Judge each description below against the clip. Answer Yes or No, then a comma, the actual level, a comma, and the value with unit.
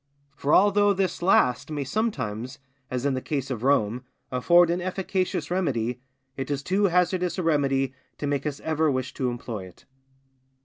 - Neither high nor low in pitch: Yes, medium, 145 Hz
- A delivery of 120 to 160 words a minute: No, average, 170 wpm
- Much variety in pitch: Yes, wide, 5.9 semitones